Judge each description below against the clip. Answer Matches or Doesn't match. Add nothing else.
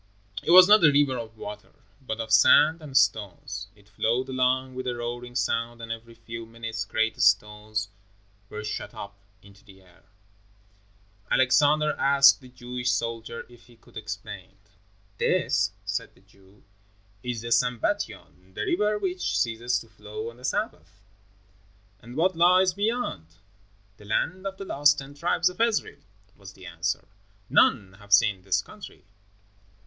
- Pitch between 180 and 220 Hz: Doesn't match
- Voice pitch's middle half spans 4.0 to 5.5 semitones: Matches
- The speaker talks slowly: Doesn't match